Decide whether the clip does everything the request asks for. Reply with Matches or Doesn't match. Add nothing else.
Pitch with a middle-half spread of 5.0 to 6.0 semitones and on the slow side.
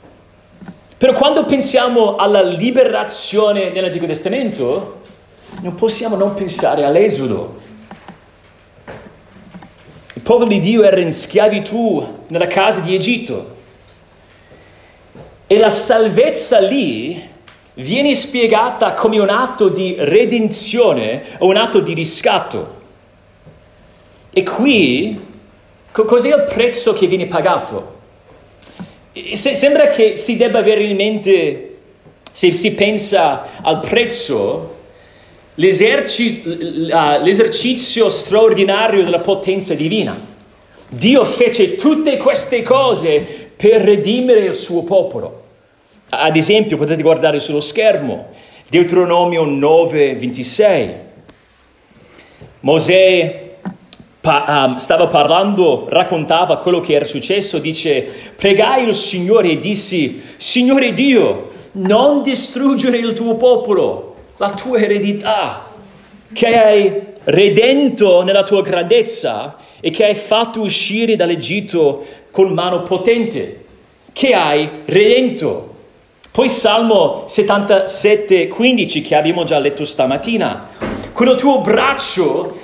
Matches